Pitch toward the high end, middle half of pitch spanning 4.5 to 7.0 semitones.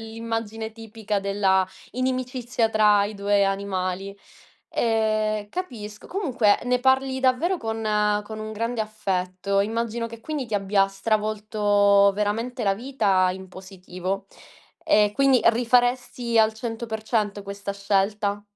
No: high, 215 Hz; average, 2.7 semitones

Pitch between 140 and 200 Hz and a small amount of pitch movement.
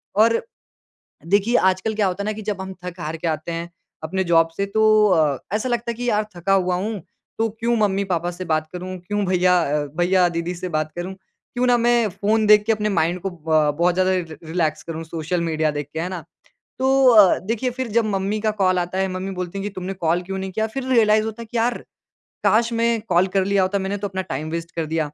No: high, 190 Hz; average, 3.8 semitones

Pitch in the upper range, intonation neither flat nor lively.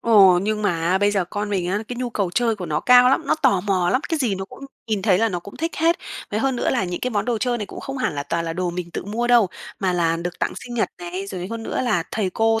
Yes: high, 205 Hz; average, 4.9 semitones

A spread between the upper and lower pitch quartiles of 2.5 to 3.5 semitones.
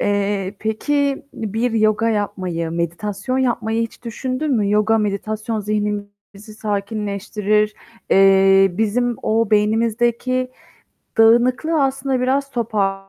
Yes: average, 2.8 semitones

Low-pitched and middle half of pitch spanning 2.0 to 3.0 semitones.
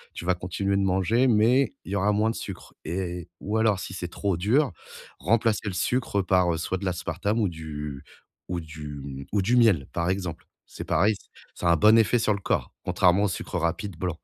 No: very low, 95 Hz; average, 3.6 semitones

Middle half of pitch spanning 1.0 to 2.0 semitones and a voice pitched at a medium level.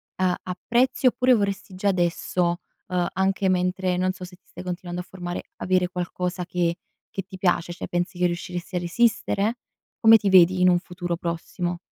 Yes: narrow, 1.4 semitones; medium, 180 Hz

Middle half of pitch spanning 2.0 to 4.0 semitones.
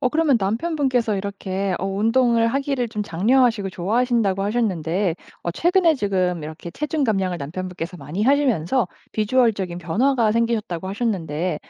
No: average, 5.2 semitones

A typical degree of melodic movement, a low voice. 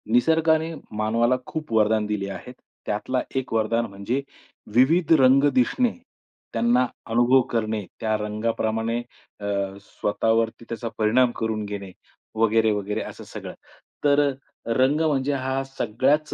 Yes: average, 3.6 semitones; low, 115 Hz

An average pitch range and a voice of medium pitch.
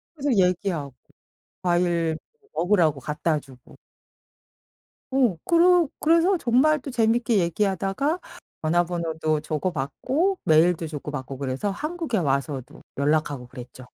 No: wide, 8.7 semitones; medium, 175 Hz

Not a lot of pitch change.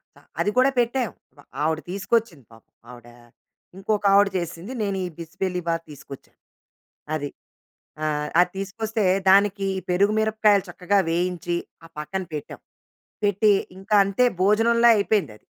No: average, 4.0 semitones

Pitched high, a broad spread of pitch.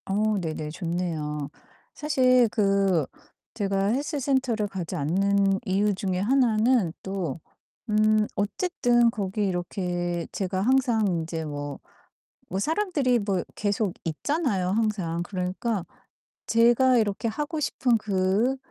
No: high, 200 Hz; average, 4.7 semitones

